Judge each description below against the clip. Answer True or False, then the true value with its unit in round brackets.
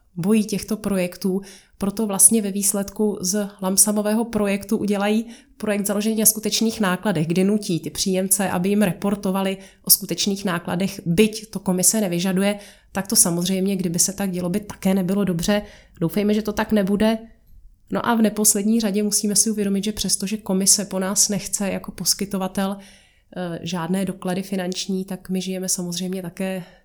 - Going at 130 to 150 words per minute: False (160 wpm)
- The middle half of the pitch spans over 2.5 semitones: False (1.9 semitones)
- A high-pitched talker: True (195 Hz)